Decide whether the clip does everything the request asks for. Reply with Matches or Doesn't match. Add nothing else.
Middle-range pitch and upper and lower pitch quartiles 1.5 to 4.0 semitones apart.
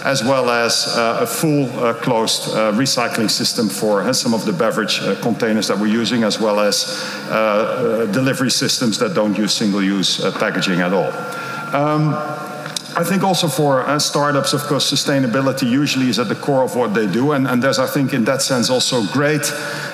Matches